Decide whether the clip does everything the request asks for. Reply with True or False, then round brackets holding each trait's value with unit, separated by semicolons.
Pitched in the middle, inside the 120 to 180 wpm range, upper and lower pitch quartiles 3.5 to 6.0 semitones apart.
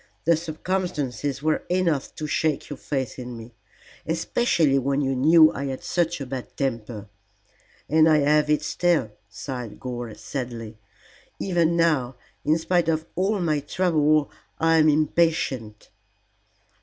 True (150 Hz; 140 wpm; 4.0 semitones)